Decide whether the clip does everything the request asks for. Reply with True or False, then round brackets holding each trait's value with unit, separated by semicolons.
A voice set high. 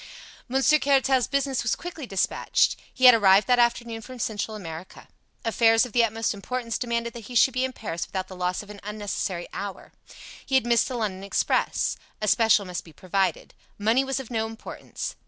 True (225 Hz)